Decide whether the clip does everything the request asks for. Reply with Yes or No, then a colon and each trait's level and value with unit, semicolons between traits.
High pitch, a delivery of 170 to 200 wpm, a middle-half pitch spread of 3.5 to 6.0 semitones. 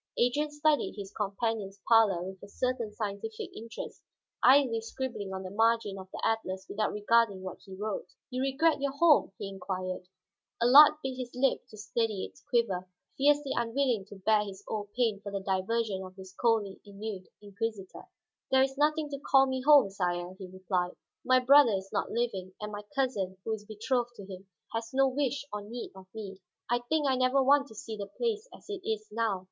Yes: high, 220 Hz; average, 195 wpm; average, 4.8 semitones